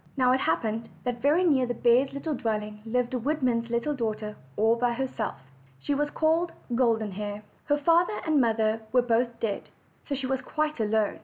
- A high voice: Yes, high, 245 Hz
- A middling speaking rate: Yes, average, 180 wpm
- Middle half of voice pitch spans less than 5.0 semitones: Yes, average, 4.1 semitones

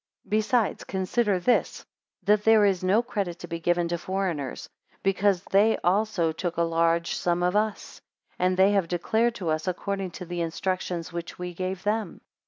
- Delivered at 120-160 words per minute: No, average, 180 wpm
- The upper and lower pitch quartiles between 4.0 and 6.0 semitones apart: No, average, 2.9 semitones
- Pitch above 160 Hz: Yes, medium, 185 Hz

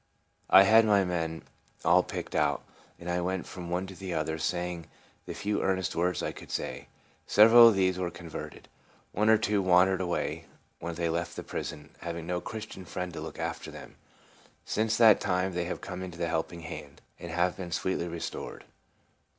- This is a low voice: Yes, very low, 90 Hz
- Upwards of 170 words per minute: Yes, average, 190 wpm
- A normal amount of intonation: No, narrow, 2.0 semitones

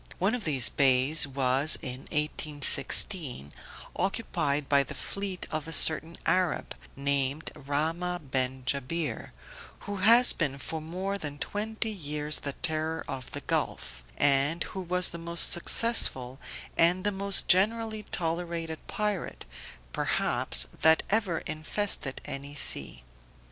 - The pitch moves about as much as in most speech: Yes, average, 4.9 semitones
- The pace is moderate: No, slow, 130 wpm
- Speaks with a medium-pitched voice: Yes, medium, 160 Hz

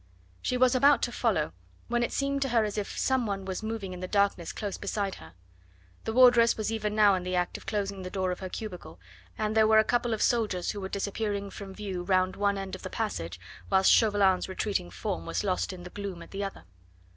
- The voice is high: Yes, high, 200 Hz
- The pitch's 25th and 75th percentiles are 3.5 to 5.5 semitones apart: No, average, 2.9 semitones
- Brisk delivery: Yes, fast, 235 wpm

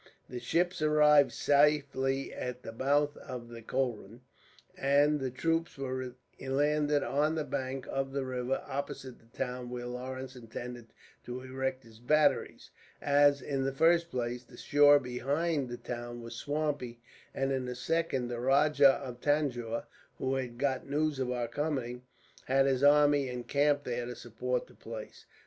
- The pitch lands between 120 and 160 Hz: Yes, low, 135 Hz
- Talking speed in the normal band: Yes, average, 160 wpm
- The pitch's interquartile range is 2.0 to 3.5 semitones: Yes, average, 2.8 semitones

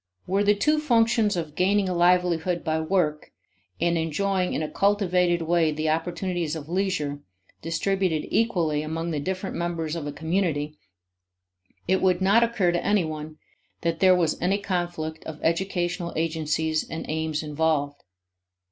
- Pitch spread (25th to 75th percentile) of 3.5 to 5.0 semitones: No, average, 3.1 semitones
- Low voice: No, medium, 170 Hz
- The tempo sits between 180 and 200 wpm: No, average, 150 wpm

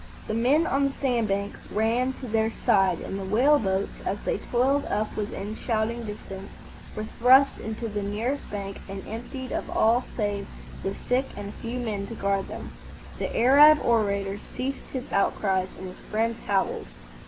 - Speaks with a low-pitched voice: No, high, 220 Hz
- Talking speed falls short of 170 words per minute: No, average, 175 wpm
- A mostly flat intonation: No, average, 3.8 semitones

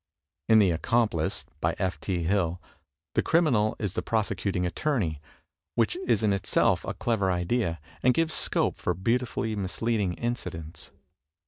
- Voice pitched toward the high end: No, low, 100 Hz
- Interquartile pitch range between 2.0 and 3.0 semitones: No, average, 4.7 semitones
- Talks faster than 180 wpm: No, average, 140 wpm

